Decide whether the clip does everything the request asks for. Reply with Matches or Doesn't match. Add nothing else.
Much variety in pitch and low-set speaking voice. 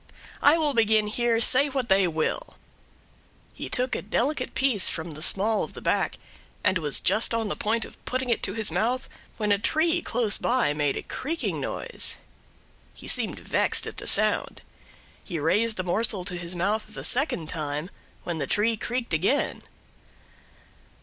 Doesn't match